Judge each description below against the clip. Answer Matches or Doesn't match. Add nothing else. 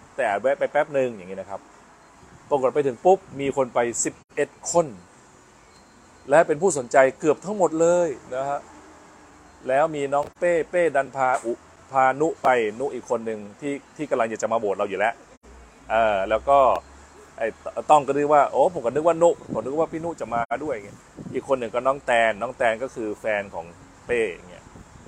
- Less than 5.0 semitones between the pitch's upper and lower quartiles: Matches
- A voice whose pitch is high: Doesn't match